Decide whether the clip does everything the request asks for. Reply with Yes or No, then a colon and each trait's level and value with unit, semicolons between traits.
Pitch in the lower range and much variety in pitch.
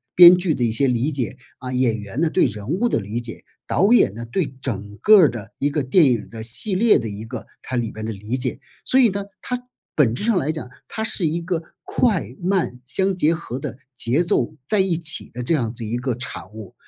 Yes: low, 130 Hz; wide, 7.5 semitones